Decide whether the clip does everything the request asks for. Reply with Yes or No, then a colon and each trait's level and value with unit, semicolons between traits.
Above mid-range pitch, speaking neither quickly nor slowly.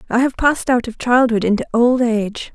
No: high, 240 Hz; fast, 210 wpm